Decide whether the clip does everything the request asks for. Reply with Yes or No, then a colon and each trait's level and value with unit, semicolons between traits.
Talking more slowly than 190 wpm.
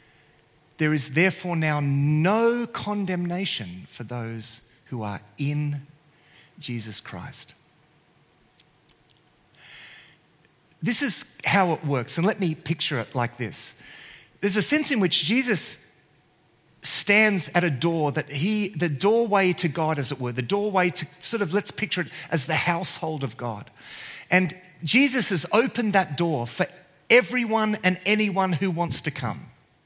Yes: average, 145 wpm